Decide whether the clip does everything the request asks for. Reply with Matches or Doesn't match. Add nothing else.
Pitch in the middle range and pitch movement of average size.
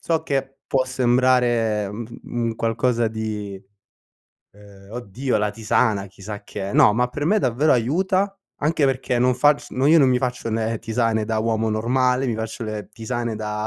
Doesn't match